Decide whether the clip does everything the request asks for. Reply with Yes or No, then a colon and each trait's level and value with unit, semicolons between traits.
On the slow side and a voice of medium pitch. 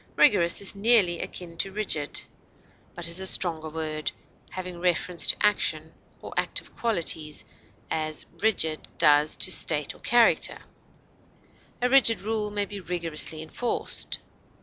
Yes: slow, 130 wpm; medium, 175 Hz